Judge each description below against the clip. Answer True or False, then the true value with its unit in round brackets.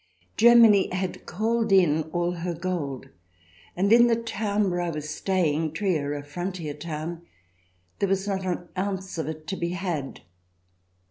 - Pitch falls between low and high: True (175 Hz)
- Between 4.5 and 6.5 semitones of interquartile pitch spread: False (3.9 semitones)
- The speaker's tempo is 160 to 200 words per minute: True (170 wpm)